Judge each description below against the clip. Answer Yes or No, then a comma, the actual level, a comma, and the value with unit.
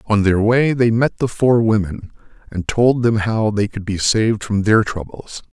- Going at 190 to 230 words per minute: Yes, fast, 205 wpm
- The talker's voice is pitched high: No, low, 110 Hz